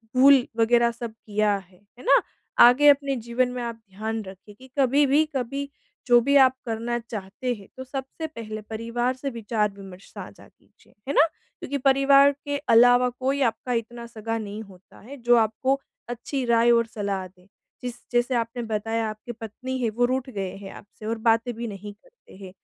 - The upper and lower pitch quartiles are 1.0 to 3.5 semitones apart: Yes, average, 3.2 semitones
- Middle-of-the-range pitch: No, high, 235 Hz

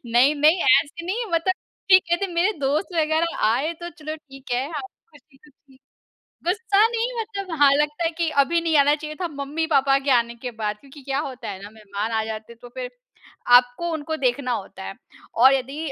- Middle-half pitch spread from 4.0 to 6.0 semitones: Yes, average, 4.9 semitones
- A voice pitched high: Yes, very high, 290 Hz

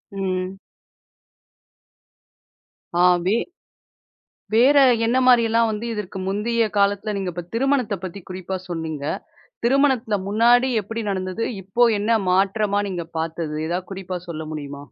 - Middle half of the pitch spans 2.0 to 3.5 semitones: No, average, 4.0 semitones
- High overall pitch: Yes, high, 200 Hz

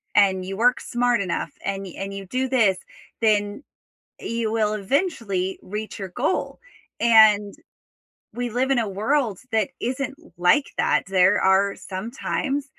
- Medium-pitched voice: No, high, 215 Hz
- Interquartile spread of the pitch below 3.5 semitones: No, average, 4.0 semitones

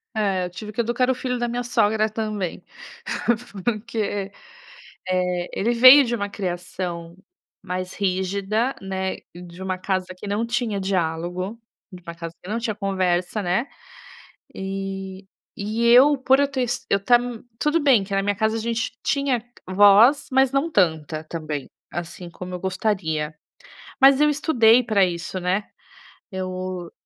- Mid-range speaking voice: No, high, 200 Hz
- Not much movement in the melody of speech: No, average, 4.4 semitones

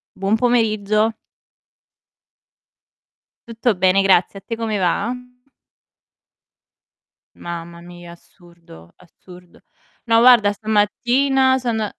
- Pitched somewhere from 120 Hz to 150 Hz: No, high, 205 Hz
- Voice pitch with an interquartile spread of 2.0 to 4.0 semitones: No, average, 4.4 semitones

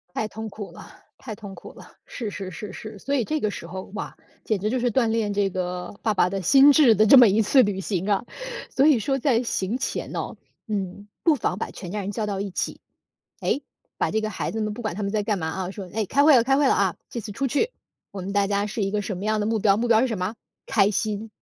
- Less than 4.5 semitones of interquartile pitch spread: Yes, average, 2.8 semitones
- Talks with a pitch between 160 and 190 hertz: No, high, 210 Hz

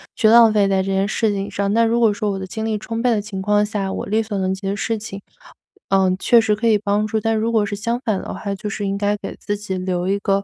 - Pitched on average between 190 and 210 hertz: Yes, high, 205 Hz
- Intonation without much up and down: Yes, narrow, 2.0 semitones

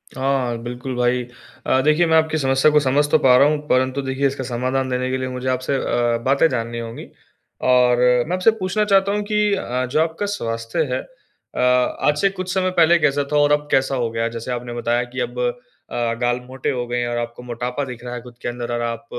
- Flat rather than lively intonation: No, average, 3.4 semitones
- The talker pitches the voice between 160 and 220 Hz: No, low, 130 Hz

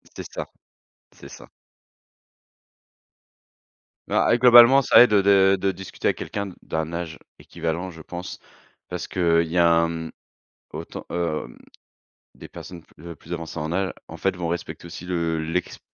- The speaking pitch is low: Yes, very low, 85 Hz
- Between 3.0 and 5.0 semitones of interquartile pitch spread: No, narrow, 2.5 semitones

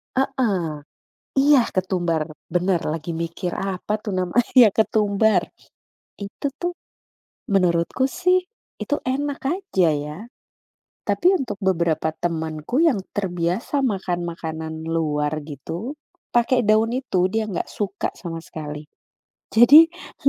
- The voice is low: No, high, 190 Hz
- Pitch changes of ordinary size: No, wide, 6.5 semitones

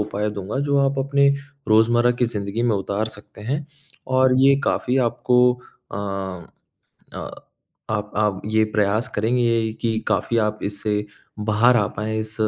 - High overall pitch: No, low, 110 Hz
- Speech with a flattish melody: No, average, 3.0 semitones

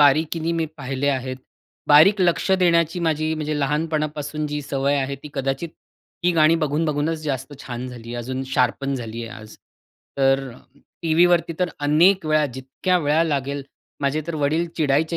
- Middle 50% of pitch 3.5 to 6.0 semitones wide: No, average, 3.1 semitones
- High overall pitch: No, medium, 150 Hz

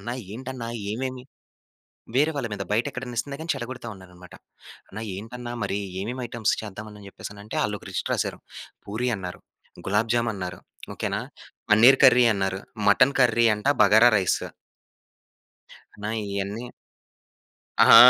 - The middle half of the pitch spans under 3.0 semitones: No, average, 3.6 semitones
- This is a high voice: No, low, 110 Hz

